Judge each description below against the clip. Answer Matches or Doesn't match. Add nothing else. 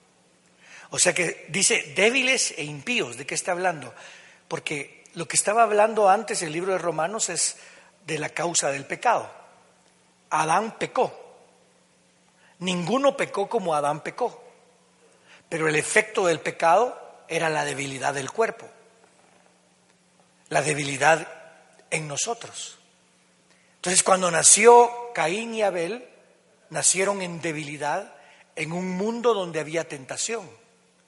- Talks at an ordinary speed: Doesn't match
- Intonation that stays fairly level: Doesn't match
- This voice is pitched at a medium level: Matches